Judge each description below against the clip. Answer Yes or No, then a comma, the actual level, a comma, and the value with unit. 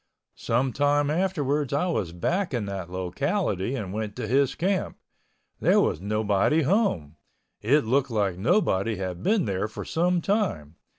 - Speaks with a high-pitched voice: No, low, 120 Hz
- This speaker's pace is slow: No, average, 155 wpm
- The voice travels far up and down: Yes, wide, 8.5 semitones